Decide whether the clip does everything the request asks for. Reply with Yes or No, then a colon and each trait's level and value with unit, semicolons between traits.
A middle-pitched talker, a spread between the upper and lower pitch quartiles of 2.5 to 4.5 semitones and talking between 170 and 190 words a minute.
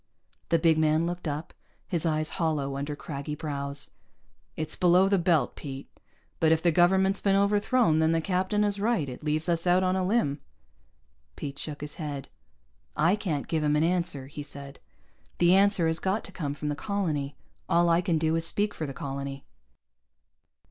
Yes: medium, 160 Hz; average, 3.8 semitones; average, 185 wpm